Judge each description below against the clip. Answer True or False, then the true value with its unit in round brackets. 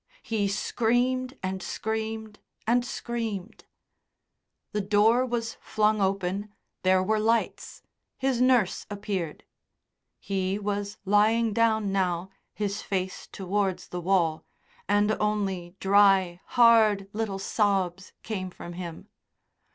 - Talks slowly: True (110 wpm)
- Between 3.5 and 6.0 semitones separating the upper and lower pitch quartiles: False (2.7 semitones)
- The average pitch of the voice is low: False (205 Hz)